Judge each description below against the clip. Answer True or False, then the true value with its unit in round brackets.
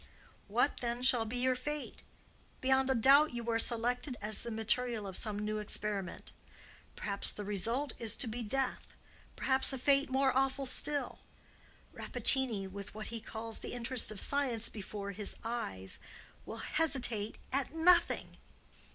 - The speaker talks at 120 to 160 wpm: True (150 wpm)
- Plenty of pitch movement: False (3.7 semitones)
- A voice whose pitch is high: True (235 Hz)